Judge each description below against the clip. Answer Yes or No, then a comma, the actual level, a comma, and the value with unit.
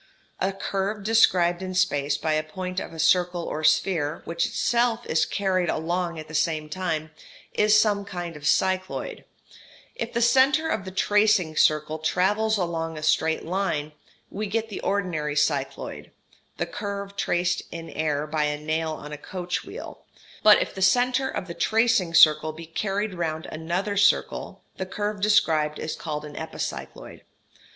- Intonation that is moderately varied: Yes, average, 4.3 semitones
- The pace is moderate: Yes, average, 165 wpm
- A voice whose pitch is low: No, medium, 180 Hz